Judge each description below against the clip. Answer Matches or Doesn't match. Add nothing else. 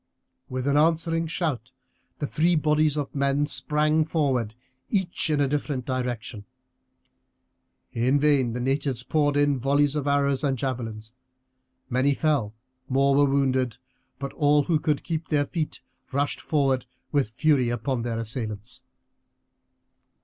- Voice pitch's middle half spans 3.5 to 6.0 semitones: Doesn't match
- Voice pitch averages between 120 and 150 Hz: Matches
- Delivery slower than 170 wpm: Matches